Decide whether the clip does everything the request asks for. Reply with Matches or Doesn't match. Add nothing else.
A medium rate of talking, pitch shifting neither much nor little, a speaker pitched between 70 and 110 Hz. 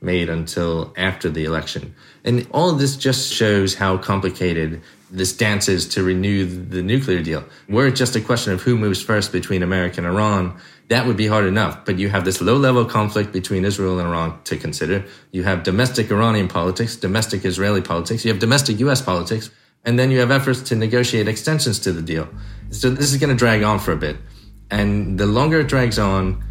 Doesn't match